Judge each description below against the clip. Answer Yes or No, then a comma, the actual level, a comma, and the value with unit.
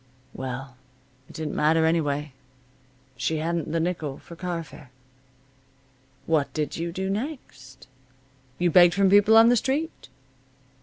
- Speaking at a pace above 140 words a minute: No, slow, 135 wpm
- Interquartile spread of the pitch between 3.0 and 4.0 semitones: No, average, 4.4 semitones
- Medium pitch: Yes, medium, 165 Hz